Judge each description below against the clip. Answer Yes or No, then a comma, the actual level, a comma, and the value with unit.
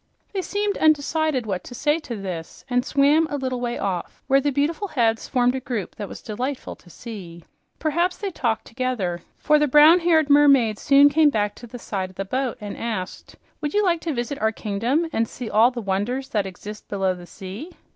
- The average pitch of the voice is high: Yes, very high, 250 Hz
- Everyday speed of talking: No, fast, 210 wpm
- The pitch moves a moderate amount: No, wide, 6.1 semitones